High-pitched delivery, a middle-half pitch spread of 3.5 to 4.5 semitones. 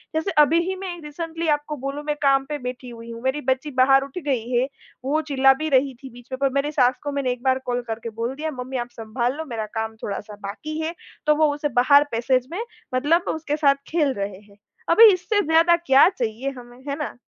Yes: very high, 275 Hz; average, 3.8 semitones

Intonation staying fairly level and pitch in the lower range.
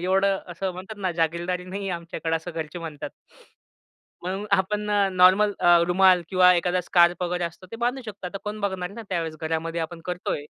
No: narrow, 2.2 semitones; medium, 180 Hz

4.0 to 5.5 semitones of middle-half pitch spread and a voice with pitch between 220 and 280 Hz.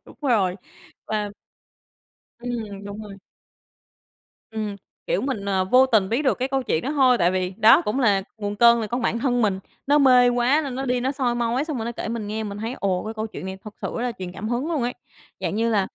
No: average, 3.6 semitones; high, 230 Hz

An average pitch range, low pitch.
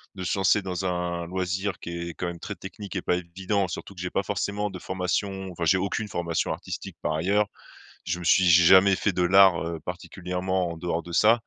No: narrow, 1.9 semitones; very low, 95 Hz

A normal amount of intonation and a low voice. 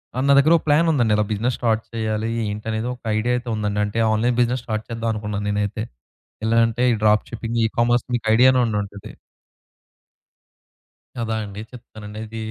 No: narrow, 2.3 semitones; low, 115 Hz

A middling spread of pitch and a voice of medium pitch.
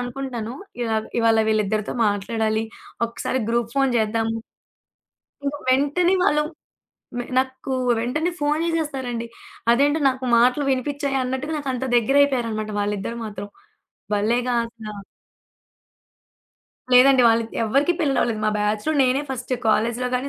No: average, 3.6 semitones; high, 245 Hz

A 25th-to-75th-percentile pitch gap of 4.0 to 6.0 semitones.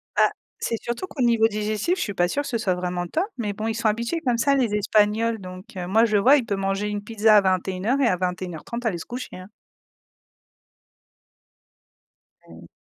No: average, 3.6 semitones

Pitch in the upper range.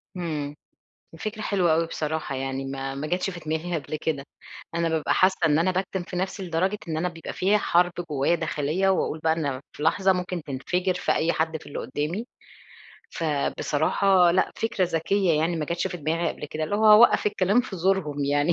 No: medium, 165 Hz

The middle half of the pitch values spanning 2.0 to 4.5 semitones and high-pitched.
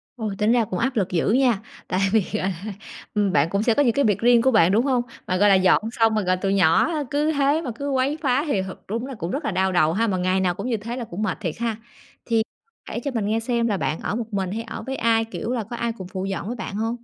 Yes: average, 4.1 semitones; high, 220 Hz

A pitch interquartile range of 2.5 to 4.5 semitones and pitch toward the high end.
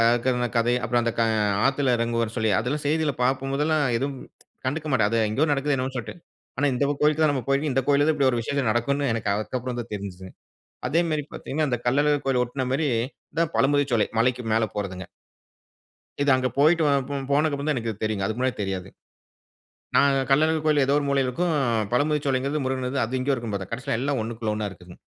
No: average, 3.6 semitones; low, 130 Hz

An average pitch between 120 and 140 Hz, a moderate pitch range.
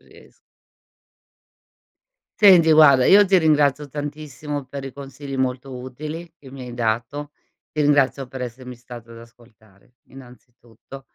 Yes: low, 135 Hz; average, 3.1 semitones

